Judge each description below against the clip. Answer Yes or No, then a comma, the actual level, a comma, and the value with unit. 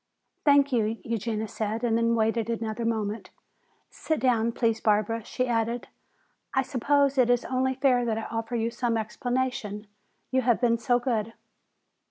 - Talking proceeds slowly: No, average, 160 wpm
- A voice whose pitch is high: Yes, high, 230 Hz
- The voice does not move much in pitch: Yes, narrow, 2.1 semitones